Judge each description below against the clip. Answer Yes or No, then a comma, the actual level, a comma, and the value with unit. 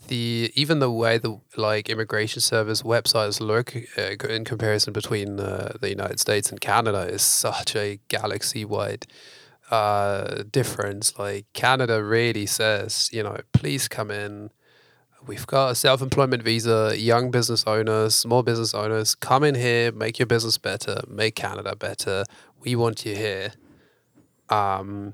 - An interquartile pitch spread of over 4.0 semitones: No, narrow, 2.4 semitones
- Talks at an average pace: Yes, average, 150 wpm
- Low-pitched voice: Yes, low, 115 Hz